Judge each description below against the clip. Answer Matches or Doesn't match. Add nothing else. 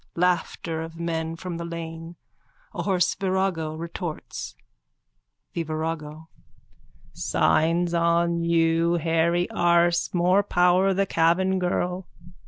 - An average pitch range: Doesn't match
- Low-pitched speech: Doesn't match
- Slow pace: Matches